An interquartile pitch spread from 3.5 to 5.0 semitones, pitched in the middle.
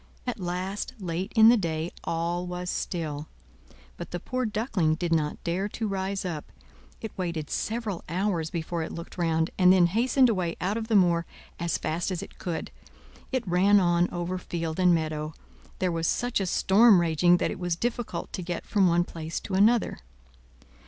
No: average, 3.1 semitones; medium, 180 Hz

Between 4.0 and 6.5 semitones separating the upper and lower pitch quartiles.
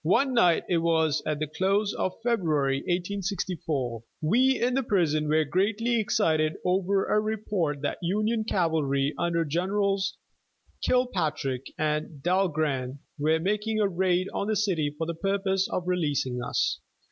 Yes: average, 4.6 semitones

